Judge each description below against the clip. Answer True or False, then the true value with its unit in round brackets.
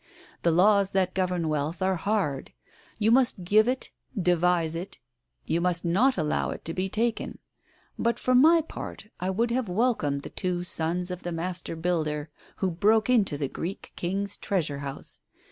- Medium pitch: True (180 Hz)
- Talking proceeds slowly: False (170 wpm)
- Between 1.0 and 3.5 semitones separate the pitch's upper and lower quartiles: False (4.2 semitones)